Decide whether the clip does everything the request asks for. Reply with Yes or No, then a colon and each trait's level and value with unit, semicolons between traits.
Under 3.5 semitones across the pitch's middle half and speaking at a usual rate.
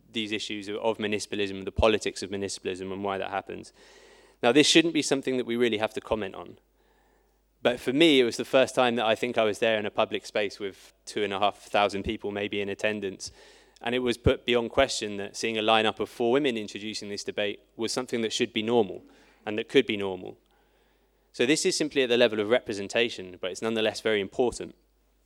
No: average, 2.9 semitones; fast, 220 wpm